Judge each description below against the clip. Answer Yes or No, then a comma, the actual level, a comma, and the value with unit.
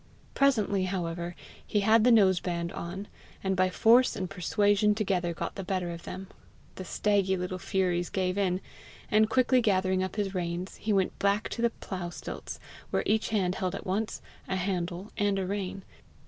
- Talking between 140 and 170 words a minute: No, average, 180 wpm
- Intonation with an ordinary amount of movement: No, narrow, 2.3 semitones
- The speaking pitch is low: No, high, 190 Hz